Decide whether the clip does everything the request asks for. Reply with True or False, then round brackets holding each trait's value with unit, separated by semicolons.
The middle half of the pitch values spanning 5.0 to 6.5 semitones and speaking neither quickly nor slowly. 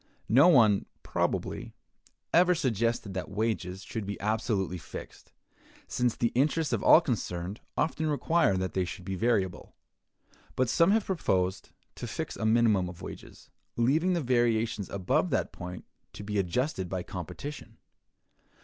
True (5.6 semitones; 145 wpm)